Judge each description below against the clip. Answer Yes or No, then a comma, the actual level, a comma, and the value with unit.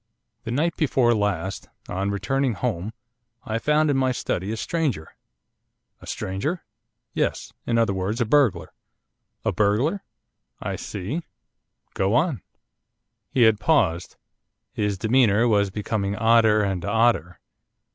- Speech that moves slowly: Yes, slow, 125 wpm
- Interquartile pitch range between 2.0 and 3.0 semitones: No, average, 4.7 semitones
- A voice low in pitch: Yes, low, 110 Hz